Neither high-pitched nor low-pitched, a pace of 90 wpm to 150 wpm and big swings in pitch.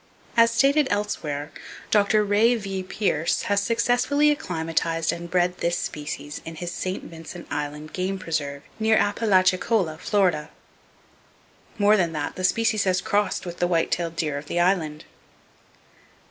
No: medium, 180 Hz; average, 145 wpm; average, 4.3 semitones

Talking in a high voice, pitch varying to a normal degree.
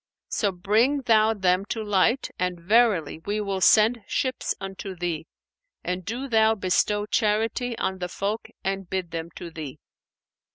Yes: high, 200 Hz; average, 3.5 semitones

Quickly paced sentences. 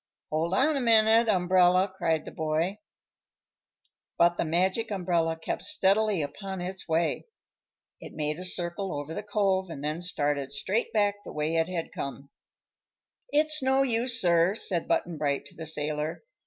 No: average, 160 wpm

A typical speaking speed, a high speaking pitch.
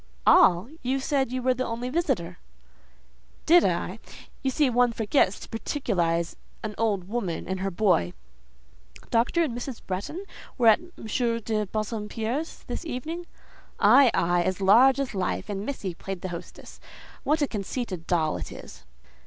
Yes: average, 155 wpm; high, 225 Hz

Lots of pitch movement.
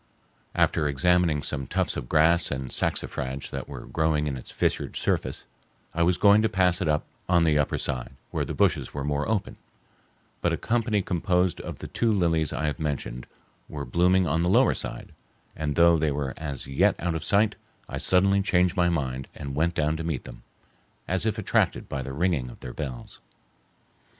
No: average, 4.1 semitones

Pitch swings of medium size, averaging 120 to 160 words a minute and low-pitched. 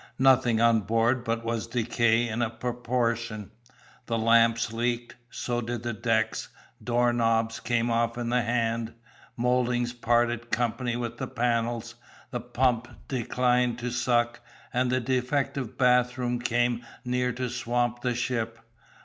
No: narrow, 1.1 semitones; average, 140 wpm; low, 120 Hz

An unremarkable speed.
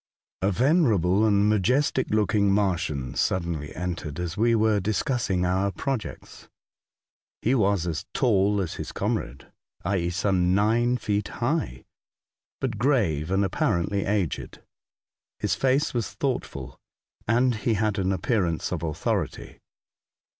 No: slow, 125 wpm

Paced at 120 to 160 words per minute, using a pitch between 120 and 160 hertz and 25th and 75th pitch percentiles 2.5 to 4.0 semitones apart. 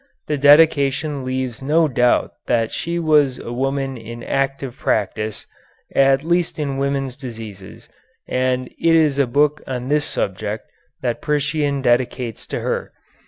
Yes: average, 140 wpm; low, 135 Hz; average, 3.2 semitones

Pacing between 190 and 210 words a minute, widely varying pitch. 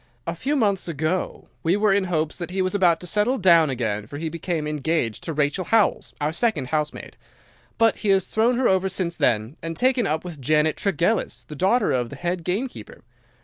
No: fast, 205 wpm; average, 4.5 semitones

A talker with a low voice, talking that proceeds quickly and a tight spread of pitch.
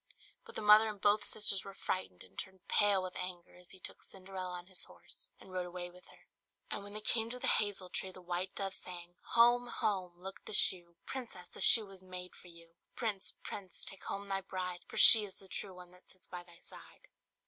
No: medium, 185 Hz; fast, 235 wpm; narrow, 2.1 semitones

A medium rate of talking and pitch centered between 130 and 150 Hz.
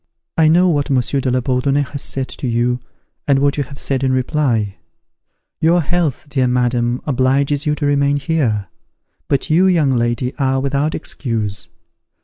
Yes: average, 165 wpm; low, 135 Hz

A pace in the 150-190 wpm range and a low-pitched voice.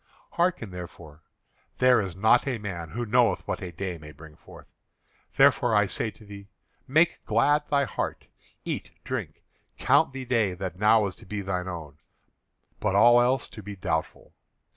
Yes: average, 170 wpm; low, 105 Hz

